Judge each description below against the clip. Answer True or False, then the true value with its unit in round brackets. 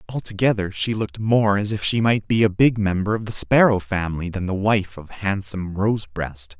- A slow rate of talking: False (200 wpm)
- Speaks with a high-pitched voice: False (100 Hz)